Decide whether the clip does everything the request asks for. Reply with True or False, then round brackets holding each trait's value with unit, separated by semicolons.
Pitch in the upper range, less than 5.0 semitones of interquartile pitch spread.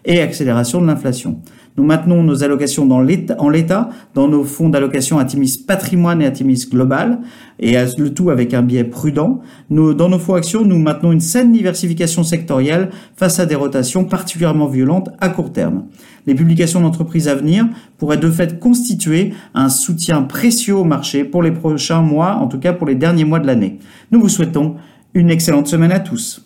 False (165 Hz; 4.5 semitones)